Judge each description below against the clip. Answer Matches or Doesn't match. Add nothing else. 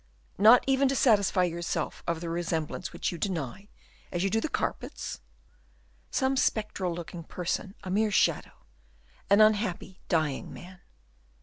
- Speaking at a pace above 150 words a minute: Doesn't match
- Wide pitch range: Doesn't match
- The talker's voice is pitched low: Doesn't match